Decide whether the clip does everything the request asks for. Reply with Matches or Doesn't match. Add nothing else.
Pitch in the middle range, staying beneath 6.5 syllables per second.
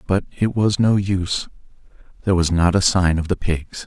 Doesn't match